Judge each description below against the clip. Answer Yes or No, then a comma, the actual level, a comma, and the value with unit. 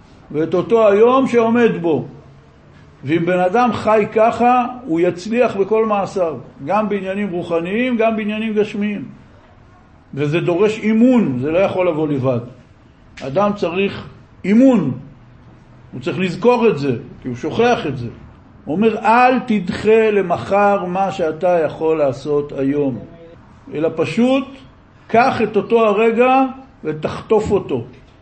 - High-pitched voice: Yes, high, 195 Hz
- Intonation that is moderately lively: No, wide, 6.2 semitones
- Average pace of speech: Yes, average, 125 wpm